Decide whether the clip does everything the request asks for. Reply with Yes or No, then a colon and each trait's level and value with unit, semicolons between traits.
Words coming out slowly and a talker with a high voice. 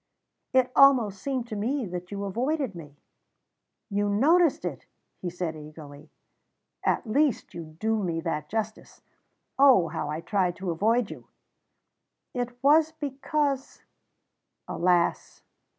Yes: slow, 130 wpm; high, 210 Hz